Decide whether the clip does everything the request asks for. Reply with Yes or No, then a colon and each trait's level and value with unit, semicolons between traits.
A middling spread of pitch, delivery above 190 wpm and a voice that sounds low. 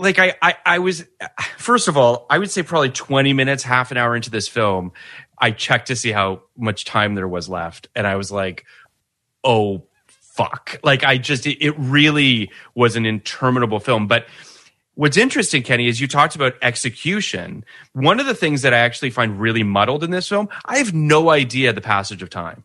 No: wide, 5.7 semitones; average, 200 wpm; low, 130 Hz